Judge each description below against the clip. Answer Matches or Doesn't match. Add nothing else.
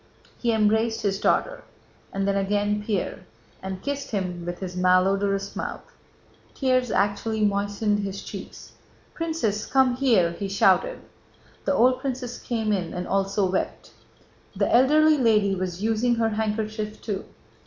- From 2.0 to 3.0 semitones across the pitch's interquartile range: Doesn't match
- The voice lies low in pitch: Doesn't match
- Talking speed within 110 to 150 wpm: Matches